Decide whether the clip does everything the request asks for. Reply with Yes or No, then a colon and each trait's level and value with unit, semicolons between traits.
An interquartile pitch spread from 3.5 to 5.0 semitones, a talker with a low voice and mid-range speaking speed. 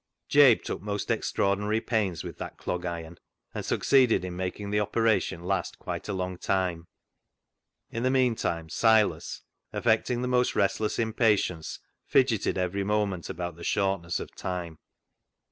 Yes: average, 3.8 semitones; low, 100 Hz; average, 145 wpm